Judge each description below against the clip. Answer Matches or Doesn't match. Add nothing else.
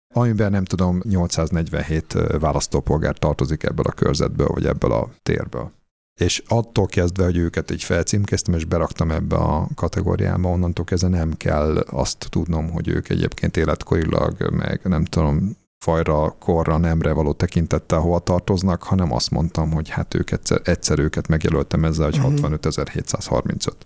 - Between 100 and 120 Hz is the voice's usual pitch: Doesn't match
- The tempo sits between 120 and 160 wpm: Matches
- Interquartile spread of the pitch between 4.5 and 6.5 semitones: Doesn't match